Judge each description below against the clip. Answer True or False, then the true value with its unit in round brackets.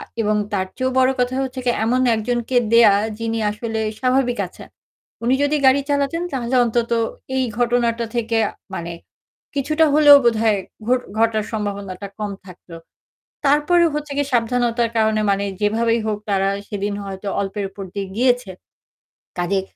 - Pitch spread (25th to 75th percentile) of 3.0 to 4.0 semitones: True (3.6 semitones)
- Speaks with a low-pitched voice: False (230 Hz)